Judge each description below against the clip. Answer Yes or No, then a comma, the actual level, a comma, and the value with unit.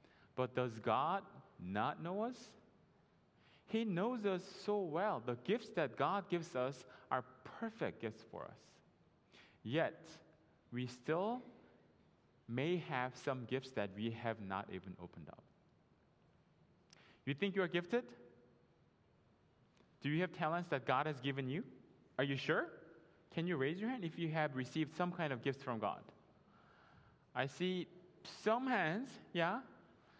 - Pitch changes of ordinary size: No, wide, 6.6 semitones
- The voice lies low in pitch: No, medium, 155 Hz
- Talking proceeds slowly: No, average, 145 wpm